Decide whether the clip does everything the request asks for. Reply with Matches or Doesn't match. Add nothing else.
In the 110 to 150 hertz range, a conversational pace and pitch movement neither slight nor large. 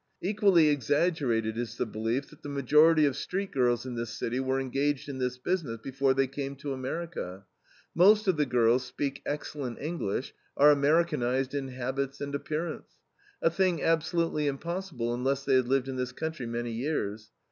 Matches